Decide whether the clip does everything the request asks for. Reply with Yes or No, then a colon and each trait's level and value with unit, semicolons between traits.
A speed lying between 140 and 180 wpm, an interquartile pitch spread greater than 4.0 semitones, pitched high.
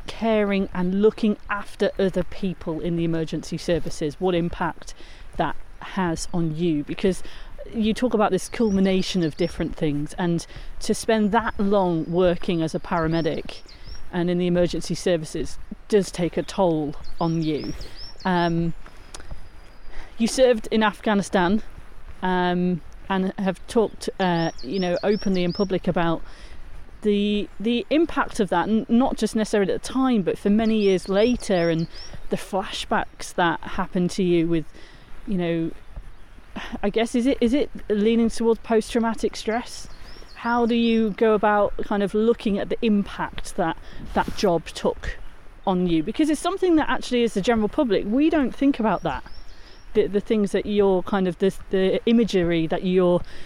Yes: average, 160 wpm; average, 4.4 semitones; high, 195 Hz